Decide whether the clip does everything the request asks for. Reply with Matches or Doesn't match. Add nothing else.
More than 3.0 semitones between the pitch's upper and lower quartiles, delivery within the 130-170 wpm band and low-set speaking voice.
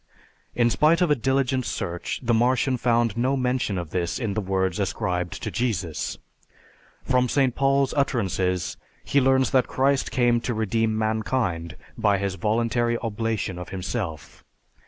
Matches